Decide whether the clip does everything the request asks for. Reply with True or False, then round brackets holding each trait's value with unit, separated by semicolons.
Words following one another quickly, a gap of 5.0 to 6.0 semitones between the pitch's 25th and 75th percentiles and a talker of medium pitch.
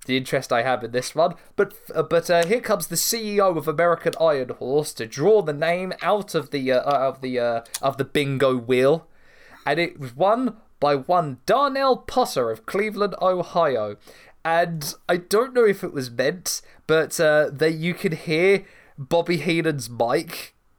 False (180 wpm; 5.5 semitones; 160 Hz)